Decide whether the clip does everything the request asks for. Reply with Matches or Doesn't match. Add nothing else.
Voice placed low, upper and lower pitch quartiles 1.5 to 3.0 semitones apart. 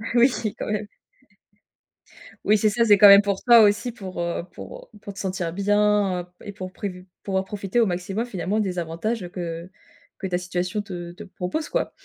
Doesn't match